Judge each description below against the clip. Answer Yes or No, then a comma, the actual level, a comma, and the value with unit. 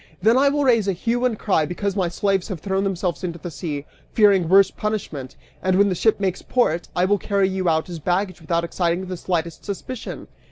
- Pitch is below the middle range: No, high, 190 Hz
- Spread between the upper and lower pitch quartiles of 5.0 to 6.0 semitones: No, average, 3.0 semitones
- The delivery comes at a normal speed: No, fast, 215 wpm